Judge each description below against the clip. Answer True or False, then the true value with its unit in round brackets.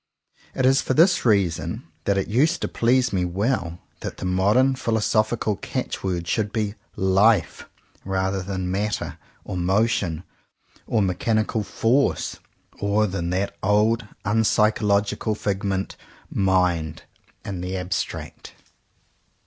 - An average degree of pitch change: True (3.0 semitones)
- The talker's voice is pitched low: True (100 Hz)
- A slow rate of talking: True (120 wpm)